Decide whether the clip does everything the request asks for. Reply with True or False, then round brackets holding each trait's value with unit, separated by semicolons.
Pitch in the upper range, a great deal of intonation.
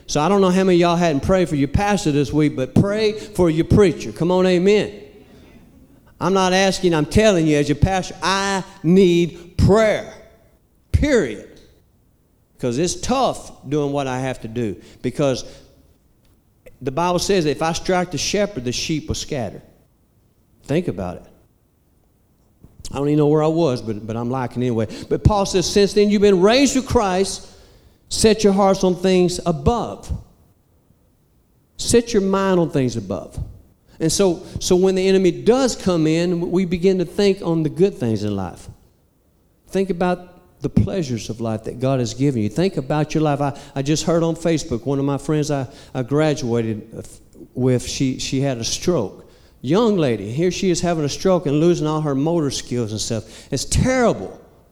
False (155 Hz; 6.9 semitones)